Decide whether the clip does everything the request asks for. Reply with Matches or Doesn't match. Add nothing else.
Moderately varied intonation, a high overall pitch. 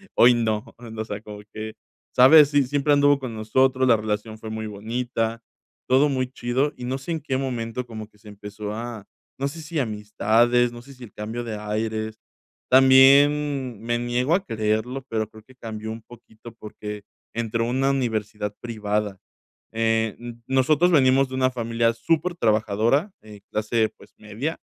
Doesn't match